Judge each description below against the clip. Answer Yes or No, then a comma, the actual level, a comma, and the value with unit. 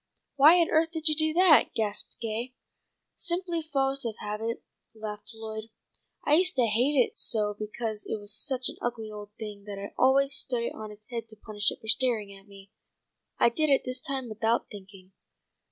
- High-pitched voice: Yes, high, 230 Hz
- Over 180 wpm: Yes, average, 195 wpm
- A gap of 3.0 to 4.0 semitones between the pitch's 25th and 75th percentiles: No, average, 4.6 semitones